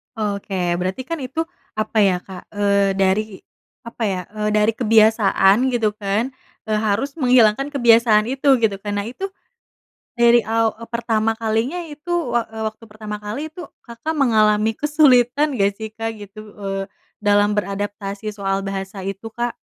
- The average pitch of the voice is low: No, high, 220 Hz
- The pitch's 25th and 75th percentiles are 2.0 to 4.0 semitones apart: Yes, average, 2.8 semitones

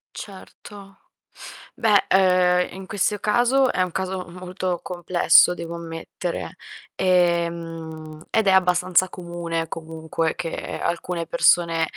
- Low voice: No, medium, 180 Hz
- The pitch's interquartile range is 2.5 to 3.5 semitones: No, narrow, 2.1 semitones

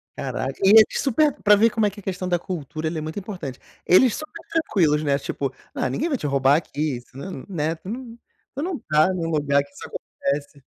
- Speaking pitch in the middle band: Yes, medium, 165 Hz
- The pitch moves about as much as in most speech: No, wide, 6.7 semitones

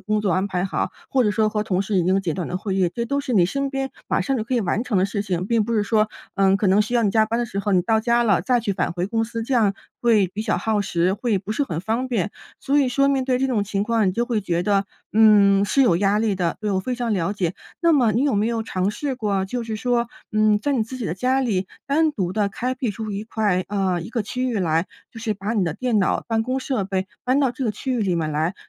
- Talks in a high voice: Yes, high, 215 Hz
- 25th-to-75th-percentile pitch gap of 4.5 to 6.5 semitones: No, average, 3.7 semitones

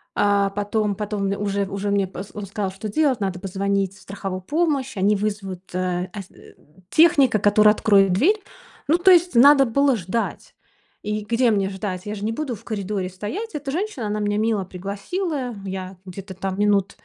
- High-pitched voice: Yes, high, 205 Hz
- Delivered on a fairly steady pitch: No, average, 3.5 semitones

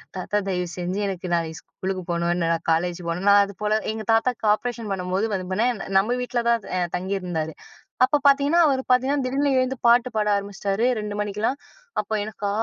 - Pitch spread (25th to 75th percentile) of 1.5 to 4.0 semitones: No, average, 4.9 semitones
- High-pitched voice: Yes, high, 205 Hz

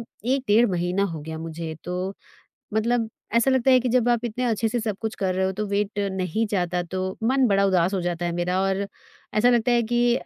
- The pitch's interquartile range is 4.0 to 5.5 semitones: Yes, average, 4.7 semitones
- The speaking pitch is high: Yes, high, 200 Hz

